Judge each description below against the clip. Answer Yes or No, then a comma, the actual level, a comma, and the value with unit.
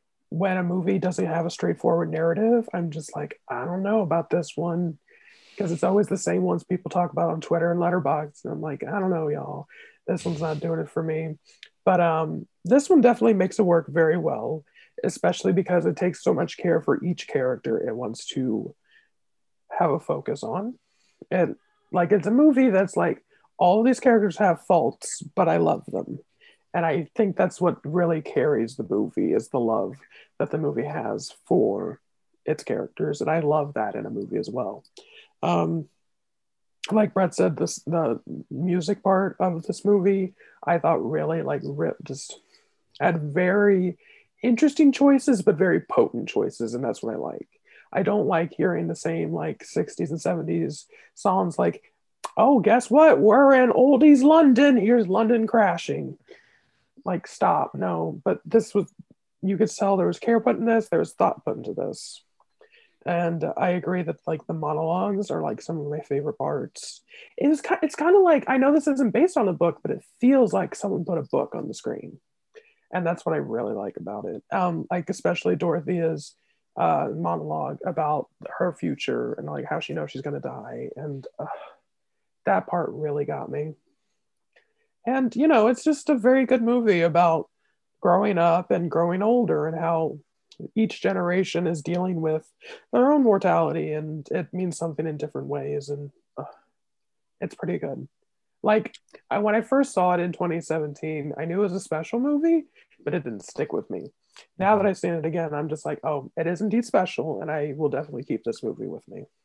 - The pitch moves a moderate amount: No, wide, 6.5 semitones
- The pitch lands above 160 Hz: Yes, medium, 185 Hz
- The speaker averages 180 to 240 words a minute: Yes, average, 185 wpm